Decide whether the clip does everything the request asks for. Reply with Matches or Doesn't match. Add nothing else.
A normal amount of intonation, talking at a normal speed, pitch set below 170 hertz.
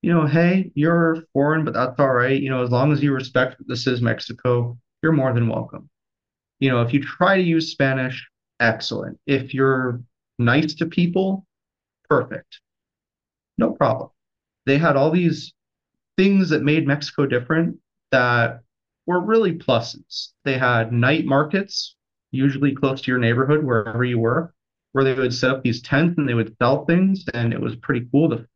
Matches